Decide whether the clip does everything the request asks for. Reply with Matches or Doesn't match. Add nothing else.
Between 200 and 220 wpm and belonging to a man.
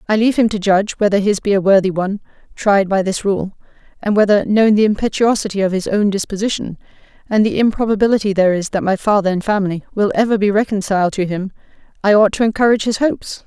Doesn't match